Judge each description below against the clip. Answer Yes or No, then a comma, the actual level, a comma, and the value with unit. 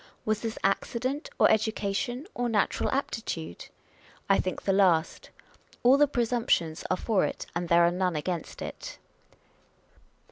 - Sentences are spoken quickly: No, average, 140 wpm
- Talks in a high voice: Yes, high, 200 Hz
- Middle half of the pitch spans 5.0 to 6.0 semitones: Yes, average, 5.3 semitones